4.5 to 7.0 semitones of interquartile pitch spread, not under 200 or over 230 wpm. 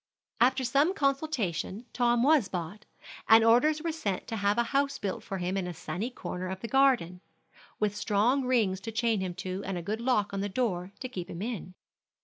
Yes: average, 5.1 semitones; fast, 205 wpm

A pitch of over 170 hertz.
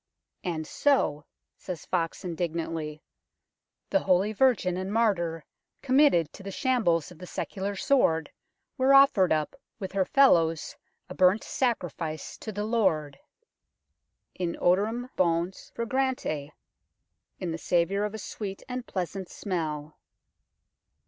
Yes: medium, 185 Hz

